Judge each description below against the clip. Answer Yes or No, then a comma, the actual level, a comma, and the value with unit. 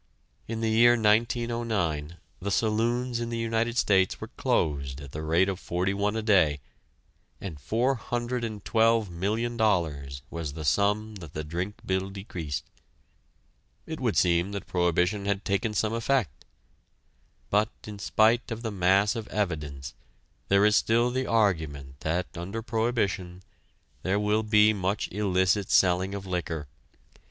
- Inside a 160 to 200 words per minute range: No, average, 140 wpm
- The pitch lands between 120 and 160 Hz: No, low, 100 Hz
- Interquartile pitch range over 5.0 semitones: No, average, 4.2 semitones